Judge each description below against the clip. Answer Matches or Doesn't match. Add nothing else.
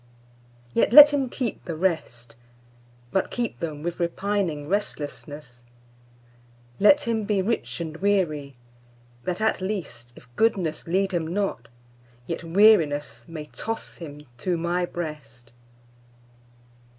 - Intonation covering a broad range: Matches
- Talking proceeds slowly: Matches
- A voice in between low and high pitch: Matches